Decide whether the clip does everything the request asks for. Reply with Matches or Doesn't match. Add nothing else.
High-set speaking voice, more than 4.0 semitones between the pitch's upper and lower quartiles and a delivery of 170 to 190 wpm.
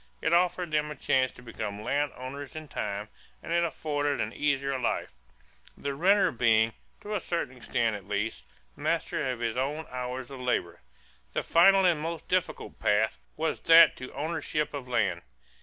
Doesn't match